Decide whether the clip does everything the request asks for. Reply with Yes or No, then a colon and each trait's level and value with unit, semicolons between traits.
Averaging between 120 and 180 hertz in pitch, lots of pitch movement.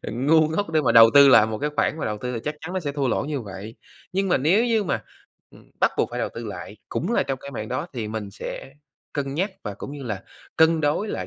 Yes: medium, 140 Hz; wide, 6.0 semitones